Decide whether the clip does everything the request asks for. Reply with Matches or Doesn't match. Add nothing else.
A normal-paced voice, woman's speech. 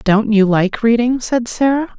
Matches